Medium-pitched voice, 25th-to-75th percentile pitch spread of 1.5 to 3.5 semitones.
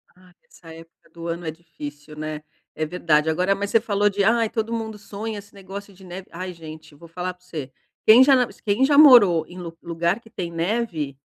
No: medium, 180 Hz; average, 4.0 semitones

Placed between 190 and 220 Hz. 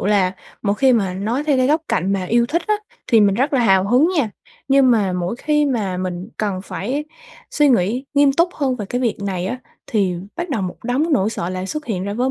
No: high, 230 Hz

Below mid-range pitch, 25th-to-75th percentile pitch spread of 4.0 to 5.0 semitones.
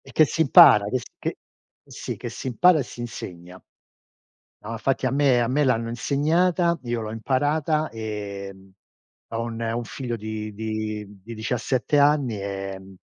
Yes: low, 115 Hz; average, 4.5 semitones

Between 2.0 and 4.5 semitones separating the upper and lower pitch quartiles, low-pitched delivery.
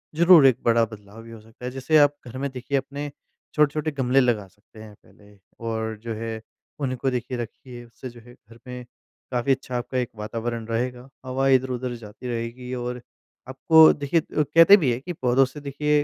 Yes: average, 2.8 semitones; low, 125 Hz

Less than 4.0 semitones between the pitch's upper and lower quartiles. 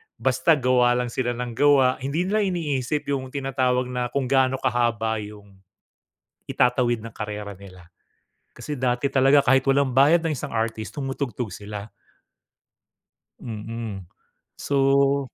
Yes: average, 3.2 semitones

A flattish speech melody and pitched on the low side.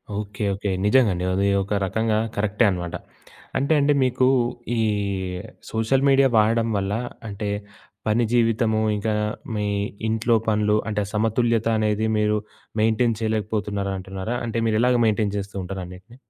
Yes: narrow, 2.1 semitones; low, 110 Hz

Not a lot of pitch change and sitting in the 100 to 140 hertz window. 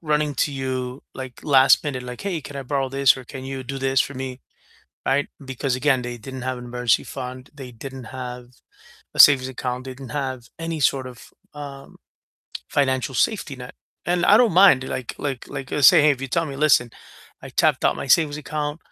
Yes: narrow, 2.2 semitones; low, 135 Hz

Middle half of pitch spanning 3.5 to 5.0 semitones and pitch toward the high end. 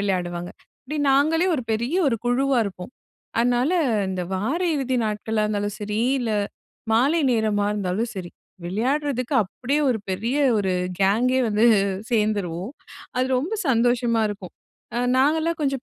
Yes: average, 4.5 semitones; high, 230 Hz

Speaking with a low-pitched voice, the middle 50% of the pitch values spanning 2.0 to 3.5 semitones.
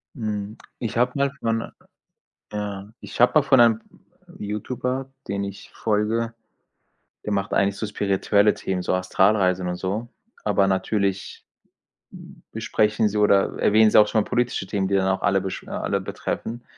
Yes: low, 105 Hz; narrow, 2.6 semitones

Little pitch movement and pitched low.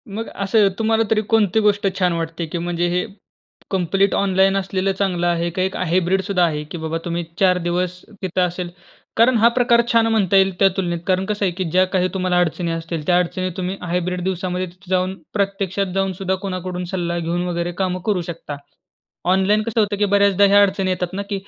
No: narrow, 2.0 semitones; medium, 185 Hz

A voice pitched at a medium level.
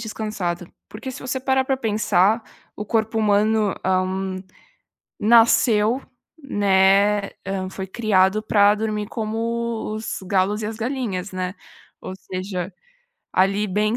No: high, 210 Hz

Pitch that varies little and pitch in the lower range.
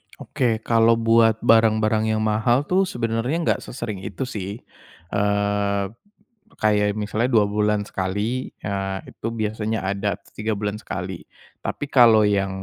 Yes: narrow, 2.0 semitones; low, 110 Hz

